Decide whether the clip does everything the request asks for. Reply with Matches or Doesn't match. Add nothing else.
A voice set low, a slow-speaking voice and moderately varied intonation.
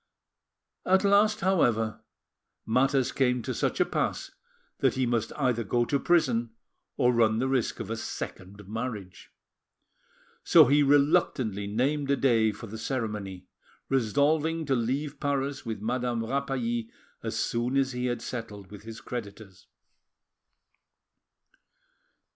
Matches